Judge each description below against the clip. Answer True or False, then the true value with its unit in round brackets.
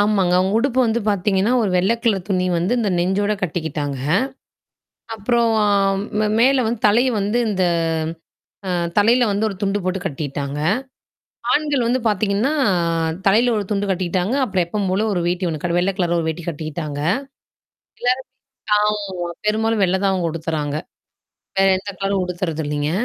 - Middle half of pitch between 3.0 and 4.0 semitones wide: True (3.5 semitones)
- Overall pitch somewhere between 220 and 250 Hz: False (195 Hz)